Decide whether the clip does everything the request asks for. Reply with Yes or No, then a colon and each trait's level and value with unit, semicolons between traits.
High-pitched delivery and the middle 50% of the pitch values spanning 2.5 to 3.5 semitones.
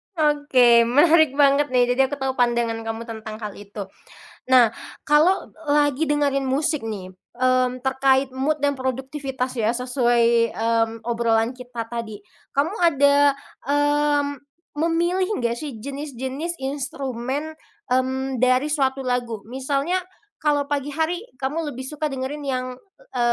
Yes: very high, 265 Hz; average, 3.2 semitones